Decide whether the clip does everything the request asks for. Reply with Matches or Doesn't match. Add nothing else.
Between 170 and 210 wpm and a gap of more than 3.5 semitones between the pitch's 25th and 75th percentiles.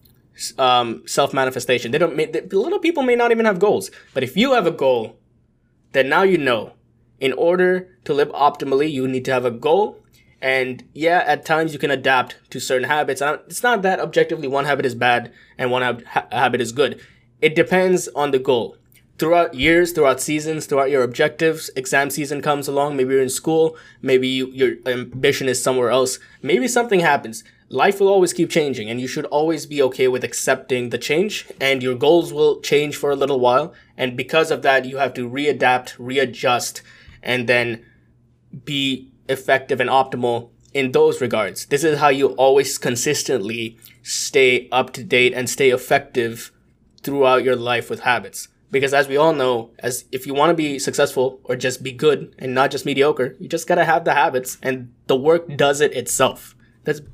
Matches